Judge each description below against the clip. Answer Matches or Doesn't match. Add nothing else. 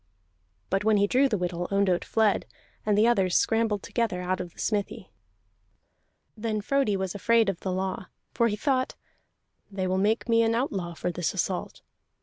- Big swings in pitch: Doesn't match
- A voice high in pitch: Matches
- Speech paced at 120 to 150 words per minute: Doesn't match